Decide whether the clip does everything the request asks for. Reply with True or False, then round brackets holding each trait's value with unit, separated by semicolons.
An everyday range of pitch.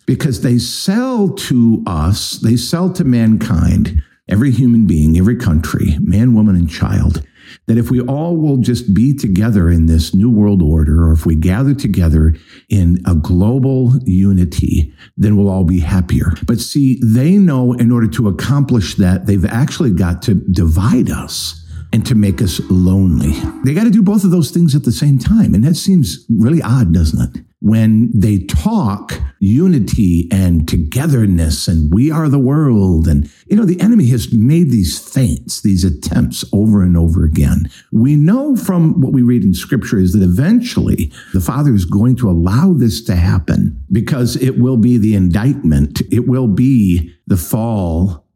False (6.6 semitones)